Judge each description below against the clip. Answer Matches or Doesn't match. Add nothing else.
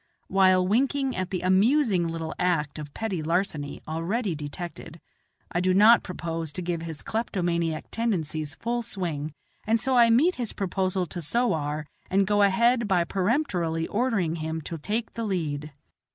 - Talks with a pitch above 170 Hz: Matches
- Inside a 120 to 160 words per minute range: Matches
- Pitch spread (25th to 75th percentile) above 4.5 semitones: Matches